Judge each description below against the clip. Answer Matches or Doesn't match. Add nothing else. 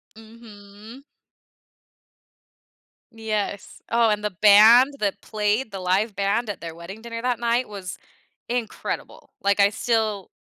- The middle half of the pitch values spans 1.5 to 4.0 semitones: Matches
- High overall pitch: Matches